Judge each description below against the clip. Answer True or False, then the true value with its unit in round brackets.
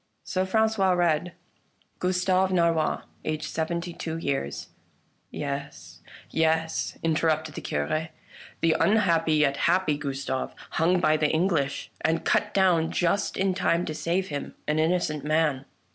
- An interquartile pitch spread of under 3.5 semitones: True (2.9 semitones)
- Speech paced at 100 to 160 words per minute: True (150 wpm)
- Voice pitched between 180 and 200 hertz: False (160 Hz)